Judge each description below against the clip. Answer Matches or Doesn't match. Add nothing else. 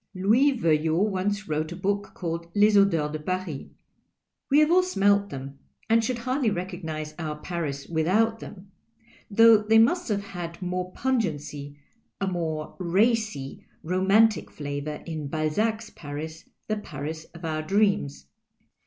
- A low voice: Doesn't match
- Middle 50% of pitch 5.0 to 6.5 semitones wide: Matches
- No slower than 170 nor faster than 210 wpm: Doesn't match